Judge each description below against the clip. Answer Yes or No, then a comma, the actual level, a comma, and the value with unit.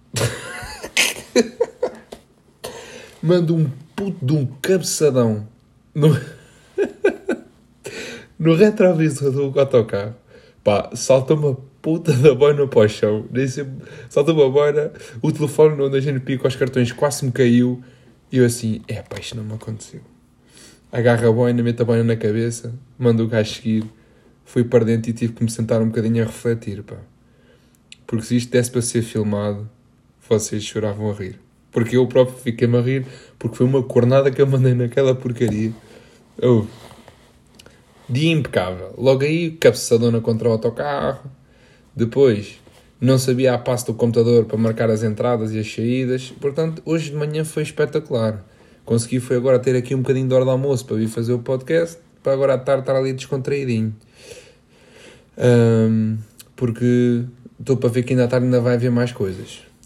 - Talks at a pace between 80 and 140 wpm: No, average, 160 wpm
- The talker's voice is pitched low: Yes, low, 125 Hz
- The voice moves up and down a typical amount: Yes, average, 3.0 semitones